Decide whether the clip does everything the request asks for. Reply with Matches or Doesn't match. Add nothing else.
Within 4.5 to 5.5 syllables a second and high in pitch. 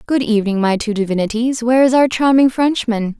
Doesn't match